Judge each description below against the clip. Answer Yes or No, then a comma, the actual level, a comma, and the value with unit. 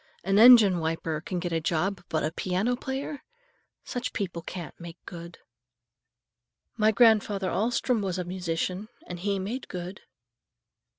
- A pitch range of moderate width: Yes, average, 4.0 semitones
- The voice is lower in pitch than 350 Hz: Yes, high, 190 Hz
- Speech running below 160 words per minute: Yes, average, 140 wpm